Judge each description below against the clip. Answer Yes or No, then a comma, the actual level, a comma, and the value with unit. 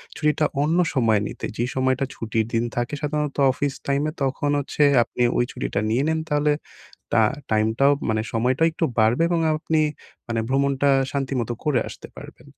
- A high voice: No, low, 135 Hz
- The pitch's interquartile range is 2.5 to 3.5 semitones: No, average, 4.1 semitones